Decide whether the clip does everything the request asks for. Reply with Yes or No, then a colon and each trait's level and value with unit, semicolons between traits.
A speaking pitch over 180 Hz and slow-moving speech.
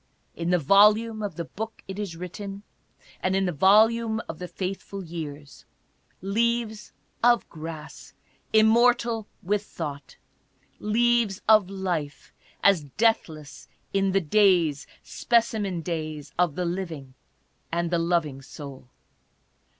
Yes: high, 190 Hz; slow, 120 wpm